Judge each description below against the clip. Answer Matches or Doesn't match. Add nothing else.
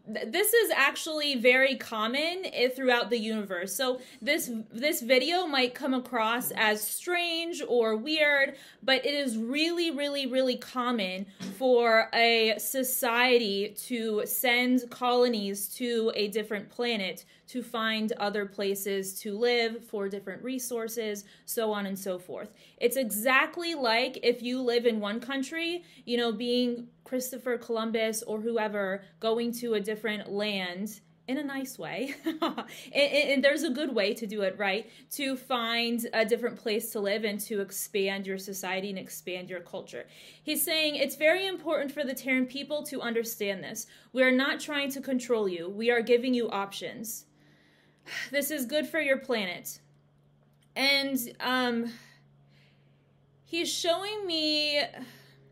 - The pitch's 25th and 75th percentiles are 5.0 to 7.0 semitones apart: Doesn't match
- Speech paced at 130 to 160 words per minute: Matches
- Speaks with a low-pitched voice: Doesn't match